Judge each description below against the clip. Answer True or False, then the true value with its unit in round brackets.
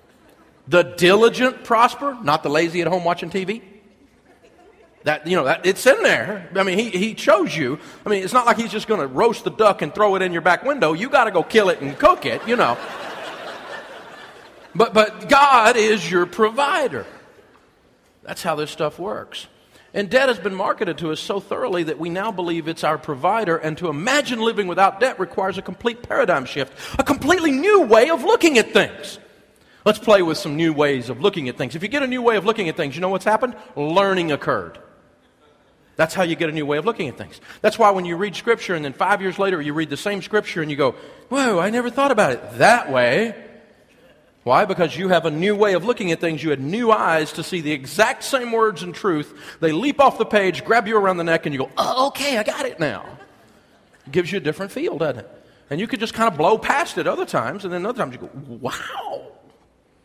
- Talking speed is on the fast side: True (230 wpm)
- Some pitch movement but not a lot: False (5.9 semitones)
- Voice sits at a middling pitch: False (195 Hz)